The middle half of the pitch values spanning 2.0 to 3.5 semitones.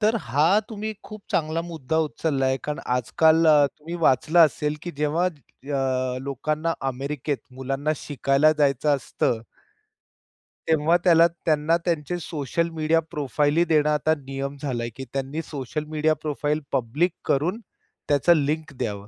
Yes: average, 2.8 semitones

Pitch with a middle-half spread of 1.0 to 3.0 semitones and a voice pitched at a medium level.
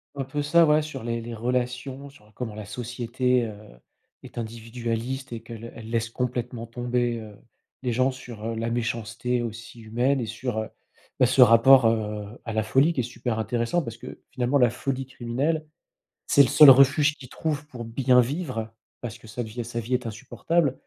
No: narrow, 2.5 semitones; low, 120 Hz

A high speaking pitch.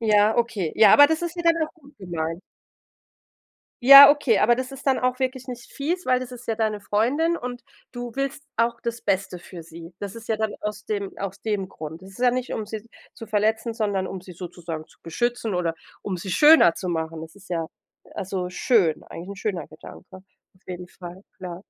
Yes: high, 210 Hz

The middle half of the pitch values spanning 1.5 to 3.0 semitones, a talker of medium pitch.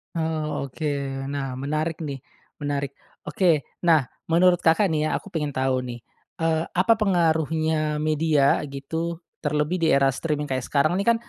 Yes: average, 2.7 semitones; medium, 155 Hz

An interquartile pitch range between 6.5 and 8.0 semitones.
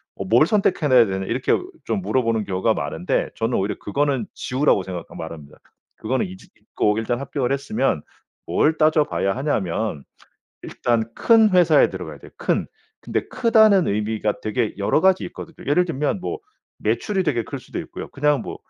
Yes: wide, 6.9 semitones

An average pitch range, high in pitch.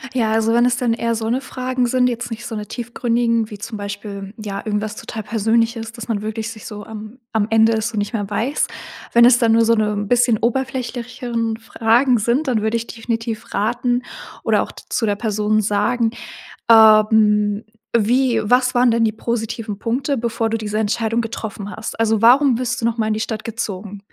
No: narrow, 1.9 semitones; high, 225 Hz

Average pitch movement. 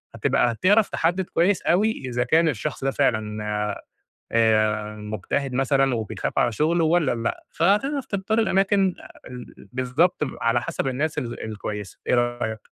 No: wide, 7.3 semitones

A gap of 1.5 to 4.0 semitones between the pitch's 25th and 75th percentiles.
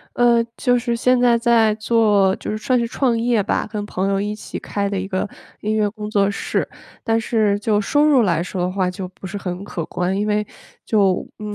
Yes: average, 2.9 semitones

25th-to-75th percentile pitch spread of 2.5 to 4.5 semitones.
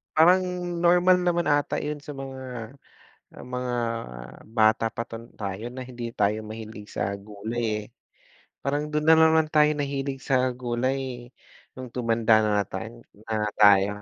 No: average, 5.1 semitones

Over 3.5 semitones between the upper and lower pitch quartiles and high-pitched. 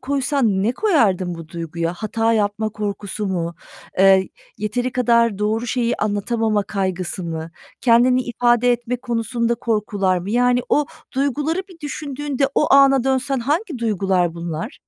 Yes: average, 4.7 semitones; high, 230 Hz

